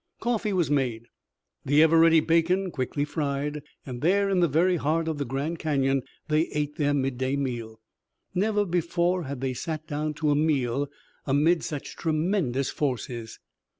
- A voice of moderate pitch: Yes, medium, 150 Hz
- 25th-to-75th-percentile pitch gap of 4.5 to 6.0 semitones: No, average, 3.6 semitones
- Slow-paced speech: No, average, 160 wpm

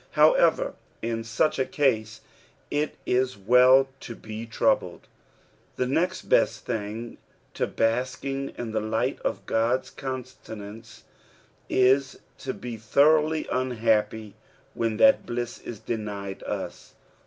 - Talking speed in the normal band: No, slow, 120 wpm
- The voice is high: No, low, 120 Hz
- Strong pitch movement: No, average, 3.2 semitones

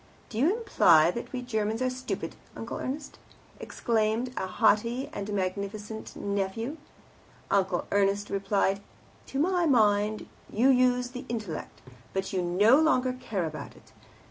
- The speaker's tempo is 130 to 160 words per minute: Yes, average, 140 wpm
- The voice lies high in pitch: Yes, high, 220 Hz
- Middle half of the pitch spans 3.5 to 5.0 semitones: Yes, average, 4.2 semitones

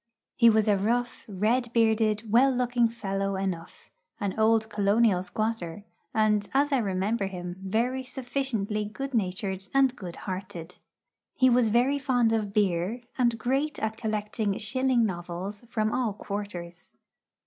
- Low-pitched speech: No, high, 215 Hz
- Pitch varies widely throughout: No, average, 3.6 semitones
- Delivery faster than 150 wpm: No, average, 140 wpm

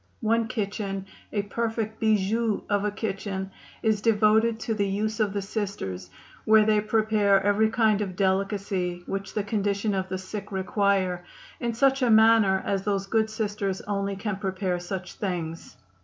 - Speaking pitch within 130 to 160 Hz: No, high, 205 Hz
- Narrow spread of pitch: Yes, narrow, 2.0 semitones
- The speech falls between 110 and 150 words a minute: No, average, 160 wpm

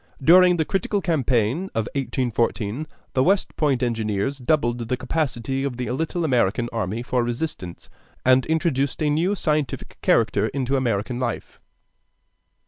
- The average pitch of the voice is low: Yes, low, 130 Hz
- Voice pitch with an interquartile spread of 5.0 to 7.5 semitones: No, average, 4.6 semitones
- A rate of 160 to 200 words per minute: No, average, 140 wpm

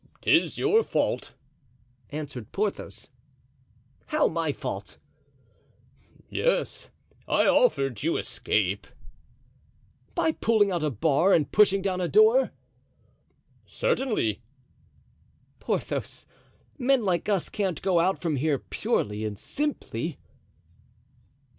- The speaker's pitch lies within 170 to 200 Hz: Yes, medium, 185 Hz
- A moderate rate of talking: No, slow, 100 wpm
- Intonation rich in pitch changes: Yes, wide, 8.6 semitones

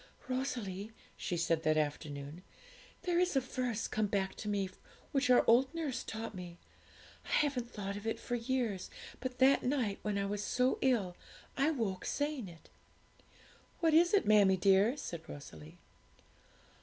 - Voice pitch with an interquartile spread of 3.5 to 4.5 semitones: No, wide, 5.4 semitones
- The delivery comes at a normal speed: Yes, average, 160 wpm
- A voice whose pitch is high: Yes, high, 220 Hz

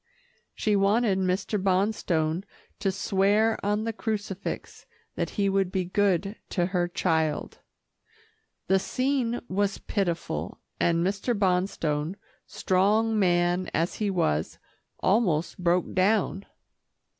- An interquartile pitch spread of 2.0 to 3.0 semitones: Yes, average, 2.7 semitones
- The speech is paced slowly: Yes, slow, 110 wpm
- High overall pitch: Yes, high, 195 Hz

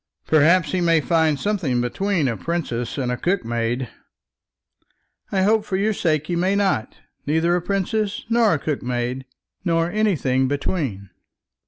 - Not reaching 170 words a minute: Yes, average, 145 wpm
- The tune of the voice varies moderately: No, wide, 6.7 semitones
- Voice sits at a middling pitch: Yes, medium, 165 Hz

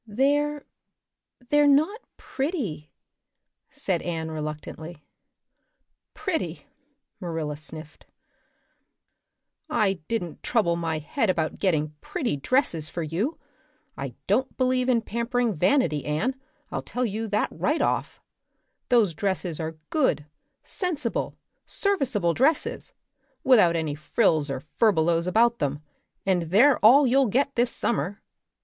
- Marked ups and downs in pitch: Yes, wide, 8.2 semitones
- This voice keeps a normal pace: No, slow, 115 wpm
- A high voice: Yes, high, 205 Hz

